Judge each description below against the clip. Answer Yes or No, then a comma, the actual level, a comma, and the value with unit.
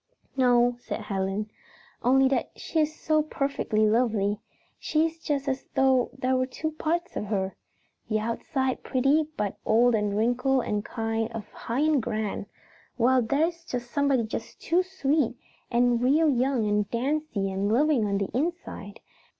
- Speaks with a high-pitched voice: Yes, high, 245 Hz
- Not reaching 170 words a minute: Yes, average, 160 wpm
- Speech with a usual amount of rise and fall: Yes, average, 4.7 semitones